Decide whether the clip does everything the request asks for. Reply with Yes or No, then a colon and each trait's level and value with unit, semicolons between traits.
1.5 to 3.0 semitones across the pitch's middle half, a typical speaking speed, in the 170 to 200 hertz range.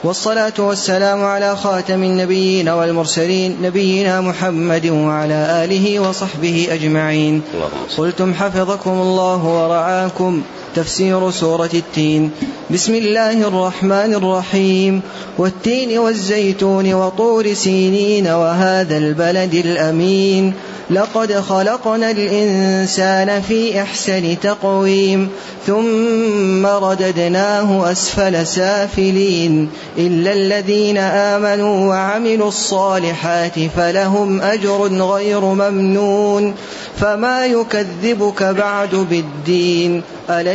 Yes: narrow, 2.4 semitones; average, 80 wpm; high, 190 Hz